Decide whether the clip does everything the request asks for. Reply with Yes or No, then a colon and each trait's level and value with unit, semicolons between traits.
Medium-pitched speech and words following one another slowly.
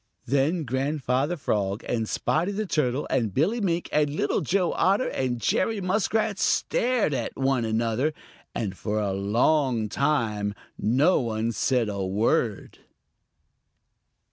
No: low, 130 Hz; slow, 130 wpm